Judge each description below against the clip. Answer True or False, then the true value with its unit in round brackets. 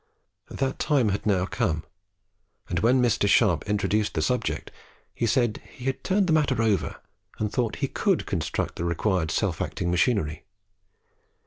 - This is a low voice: True (105 Hz)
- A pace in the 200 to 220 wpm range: False (155 wpm)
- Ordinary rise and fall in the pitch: False (6.3 semitones)